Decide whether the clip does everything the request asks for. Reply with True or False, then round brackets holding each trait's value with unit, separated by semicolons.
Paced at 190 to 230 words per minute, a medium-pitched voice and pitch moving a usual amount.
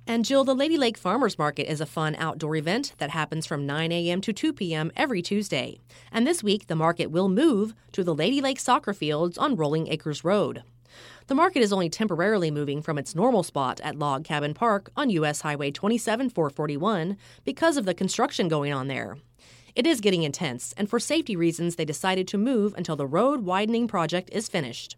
False (200 wpm; 175 Hz; 6.2 semitones)